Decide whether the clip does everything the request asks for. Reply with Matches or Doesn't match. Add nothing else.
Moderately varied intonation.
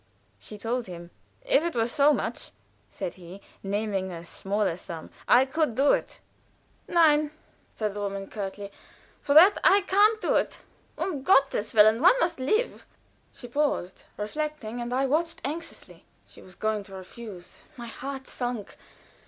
Doesn't match